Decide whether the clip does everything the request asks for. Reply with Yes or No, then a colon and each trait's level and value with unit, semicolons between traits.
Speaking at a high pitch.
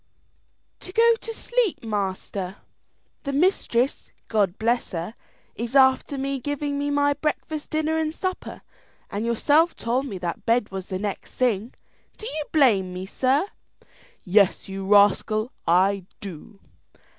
Yes: high, 235 Hz